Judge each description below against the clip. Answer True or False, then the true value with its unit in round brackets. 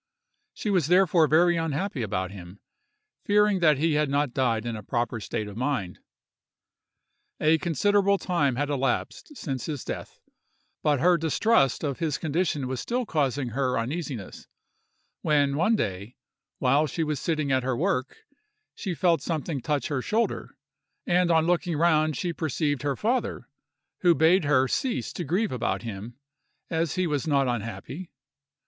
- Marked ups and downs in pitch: False (5.0 semitones)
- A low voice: False (150 Hz)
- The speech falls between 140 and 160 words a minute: True (155 wpm)